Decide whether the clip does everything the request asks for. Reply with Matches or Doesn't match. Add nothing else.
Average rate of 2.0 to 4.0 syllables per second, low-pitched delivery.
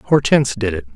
Doesn't match